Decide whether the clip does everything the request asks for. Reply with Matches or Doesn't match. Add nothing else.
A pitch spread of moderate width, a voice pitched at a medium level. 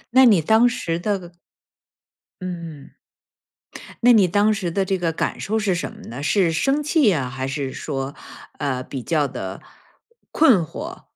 Doesn't match